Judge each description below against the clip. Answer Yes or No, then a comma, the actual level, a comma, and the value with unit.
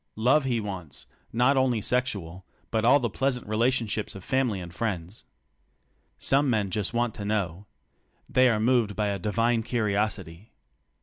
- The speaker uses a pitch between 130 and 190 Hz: No, low, 110 Hz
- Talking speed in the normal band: Yes, average, 165 wpm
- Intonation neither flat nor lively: Yes, average, 3.6 semitones